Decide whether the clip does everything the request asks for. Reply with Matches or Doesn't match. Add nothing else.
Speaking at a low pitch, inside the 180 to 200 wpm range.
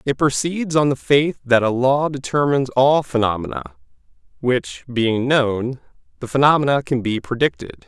Doesn't match